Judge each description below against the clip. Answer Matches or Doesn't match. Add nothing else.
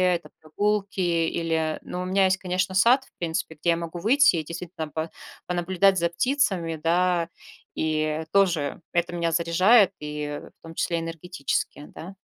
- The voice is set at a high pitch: Doesn't match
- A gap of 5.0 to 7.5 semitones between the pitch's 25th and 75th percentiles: Doesn't match